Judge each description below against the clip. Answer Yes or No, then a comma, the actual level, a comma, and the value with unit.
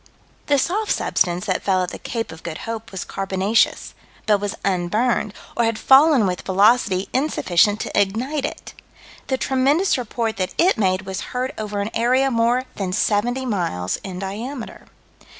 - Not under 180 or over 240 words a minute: No, average, 165 wpm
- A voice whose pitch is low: No, high, 215 Hz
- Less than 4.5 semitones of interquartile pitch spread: No, average, 5.0 semitones